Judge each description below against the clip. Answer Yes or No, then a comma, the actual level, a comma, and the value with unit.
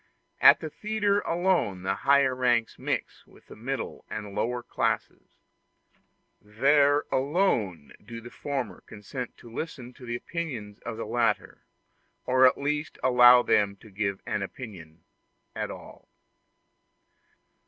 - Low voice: Yes, low, 125 Hz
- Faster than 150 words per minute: No, average, 140 wpm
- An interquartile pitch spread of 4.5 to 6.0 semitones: Yes, average, 5.0 semitones